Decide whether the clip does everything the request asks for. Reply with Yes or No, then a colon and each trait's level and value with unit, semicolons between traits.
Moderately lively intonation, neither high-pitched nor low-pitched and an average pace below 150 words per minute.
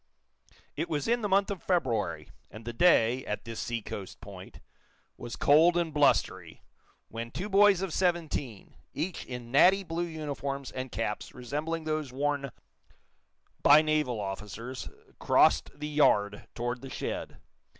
No: wide, 5.9 semitones; medium, 145 Hz; average, 140 wpm